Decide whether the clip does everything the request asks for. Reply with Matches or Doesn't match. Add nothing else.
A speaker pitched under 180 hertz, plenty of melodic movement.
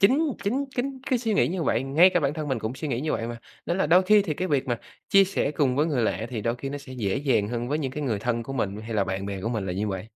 Matches